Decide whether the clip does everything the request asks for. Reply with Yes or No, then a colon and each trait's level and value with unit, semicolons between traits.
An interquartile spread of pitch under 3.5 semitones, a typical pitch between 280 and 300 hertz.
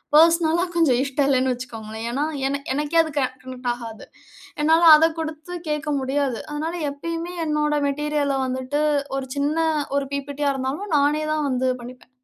Yes: average, 3.0 semitones; very high, 285 Hz